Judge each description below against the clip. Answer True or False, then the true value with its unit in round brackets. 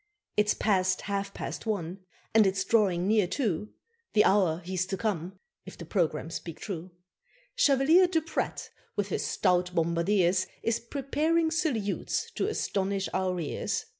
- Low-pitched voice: False (195 Hz)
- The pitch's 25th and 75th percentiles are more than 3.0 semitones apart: True (3.6 semitones)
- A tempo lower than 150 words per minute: True (140 wpm)